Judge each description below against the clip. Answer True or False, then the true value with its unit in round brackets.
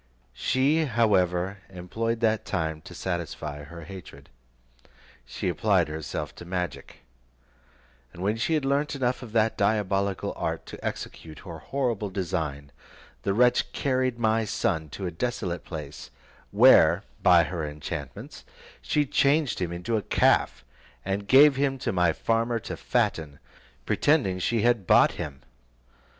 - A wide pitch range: True (5.8 semitones)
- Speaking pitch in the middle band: False (100 Hz)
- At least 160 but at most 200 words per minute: False (140 wpm)